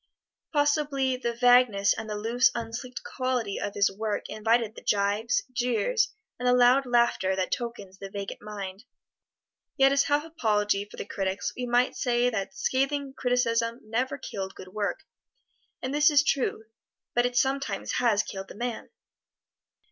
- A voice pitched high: Yes, high, 240 Hz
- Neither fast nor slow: Yes, average, 155 wpm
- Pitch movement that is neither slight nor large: Yes, average, 3.8 semitones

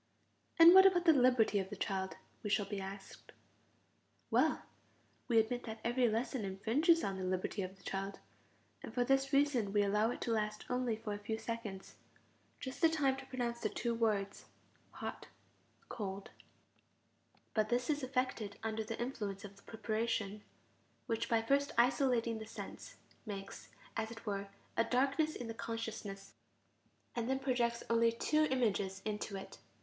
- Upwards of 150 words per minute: Yes, average, 165 wpm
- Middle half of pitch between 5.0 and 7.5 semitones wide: No, average, 3.7 semitones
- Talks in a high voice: Yes, high, 225 Hz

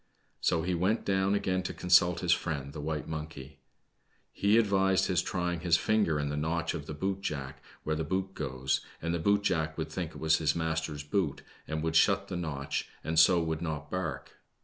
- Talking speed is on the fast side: Yes, fast, 210 wpm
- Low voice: Yes, very low, 80 Hz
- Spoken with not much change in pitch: No, average, 3.2 semitones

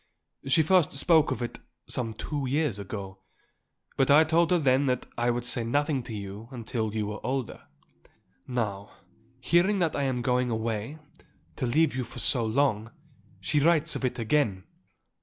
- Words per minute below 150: No, average, 170 wpm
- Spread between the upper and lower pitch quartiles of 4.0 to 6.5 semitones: Yes, average, 4.7 semitones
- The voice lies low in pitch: Yes, low, 125 Hz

